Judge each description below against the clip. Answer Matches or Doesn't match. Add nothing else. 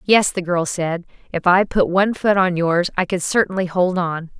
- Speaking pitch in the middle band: Matches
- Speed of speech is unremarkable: Doesn't match